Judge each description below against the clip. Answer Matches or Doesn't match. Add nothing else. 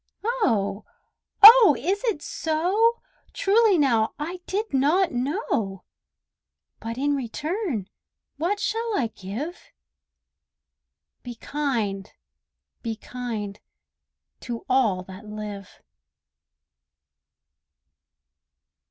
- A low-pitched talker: Doesn't match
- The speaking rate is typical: Doesn't match